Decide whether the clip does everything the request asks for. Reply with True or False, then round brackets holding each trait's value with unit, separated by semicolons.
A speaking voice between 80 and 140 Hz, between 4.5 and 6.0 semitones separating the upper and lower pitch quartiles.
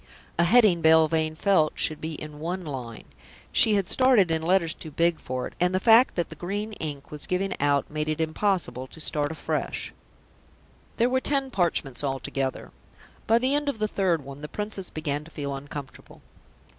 False (165 Hz; 5.1 semitones)